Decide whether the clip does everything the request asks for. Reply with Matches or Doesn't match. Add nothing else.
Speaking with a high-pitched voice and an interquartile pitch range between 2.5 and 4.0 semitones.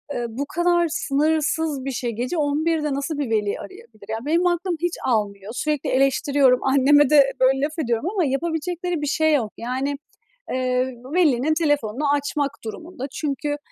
Matches